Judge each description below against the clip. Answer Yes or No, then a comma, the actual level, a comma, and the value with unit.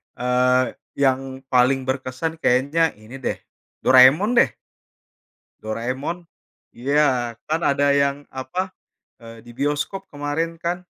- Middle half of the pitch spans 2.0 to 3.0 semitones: No, average, 3.5 semitones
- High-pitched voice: No, low, 135 Hz